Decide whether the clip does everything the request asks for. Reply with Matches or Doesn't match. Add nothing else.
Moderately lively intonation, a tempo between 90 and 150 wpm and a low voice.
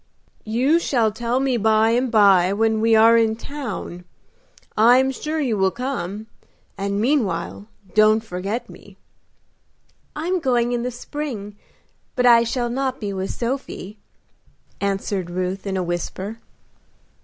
Doesn't match